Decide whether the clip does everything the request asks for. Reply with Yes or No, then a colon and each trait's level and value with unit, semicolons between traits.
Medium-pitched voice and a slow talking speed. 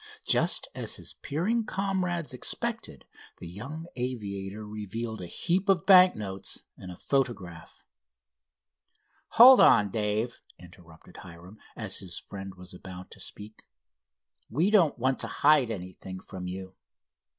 No: low, 110 Hz; slow, 130 wpm